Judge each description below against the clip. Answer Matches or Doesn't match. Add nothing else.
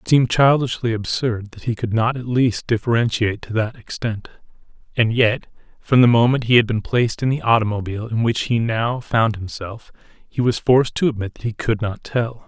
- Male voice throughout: Matches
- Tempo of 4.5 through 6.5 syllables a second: Matches